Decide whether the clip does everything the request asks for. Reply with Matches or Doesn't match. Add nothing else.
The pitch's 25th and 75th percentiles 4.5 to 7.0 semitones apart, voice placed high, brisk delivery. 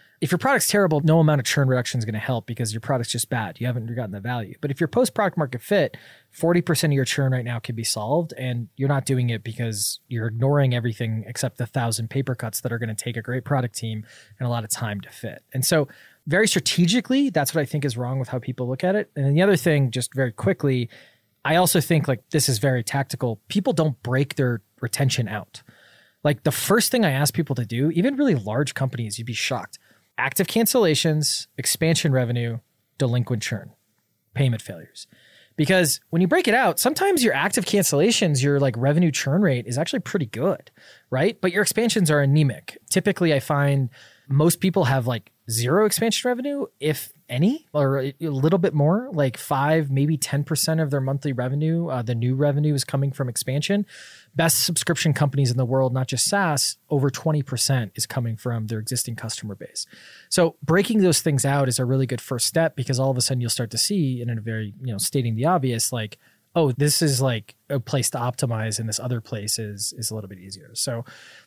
Doesn't match